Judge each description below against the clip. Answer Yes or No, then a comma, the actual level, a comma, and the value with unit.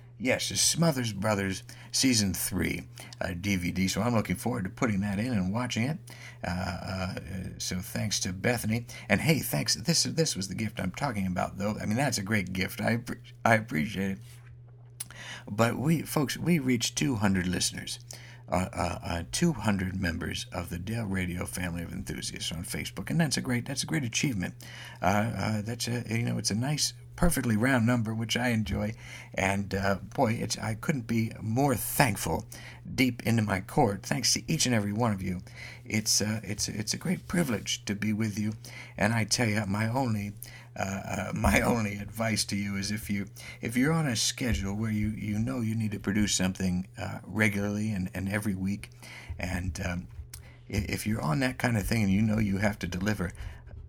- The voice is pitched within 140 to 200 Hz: No, low, 105 Hz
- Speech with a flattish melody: No, average, 3.8 semitones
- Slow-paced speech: No, average, 195 wpm